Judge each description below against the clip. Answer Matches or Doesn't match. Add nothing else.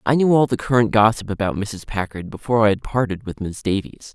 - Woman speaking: Doesn't match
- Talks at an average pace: Doesn't match